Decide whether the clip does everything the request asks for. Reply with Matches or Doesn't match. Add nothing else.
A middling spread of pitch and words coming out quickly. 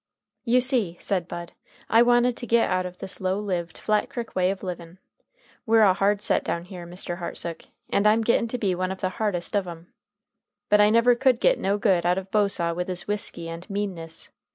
Matches